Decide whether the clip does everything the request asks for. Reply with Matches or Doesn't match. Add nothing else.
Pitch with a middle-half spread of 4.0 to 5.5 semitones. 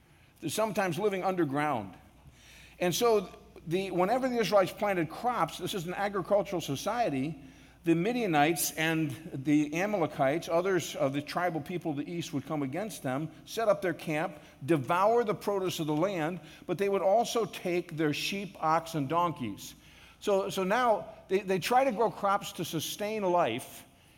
Matches